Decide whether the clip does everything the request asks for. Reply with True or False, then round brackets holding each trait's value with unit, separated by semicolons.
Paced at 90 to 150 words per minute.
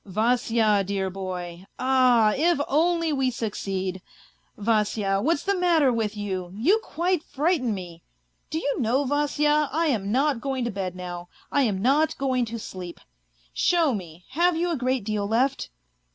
False (165 wpm)